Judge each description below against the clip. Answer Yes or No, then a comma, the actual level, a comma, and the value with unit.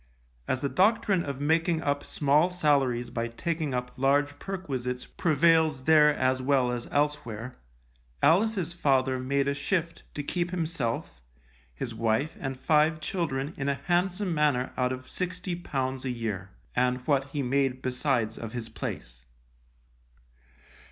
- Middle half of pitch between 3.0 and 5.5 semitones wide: Yes, average, 4.2 semitones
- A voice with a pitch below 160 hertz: Yes, medium, 140 Hz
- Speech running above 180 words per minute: No, average, 140 wpm